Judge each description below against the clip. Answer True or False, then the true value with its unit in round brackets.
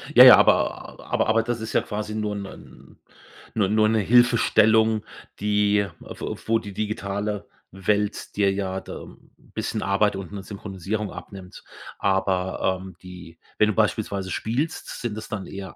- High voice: False (105 Hz)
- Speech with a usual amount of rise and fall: False (2.0 semitones)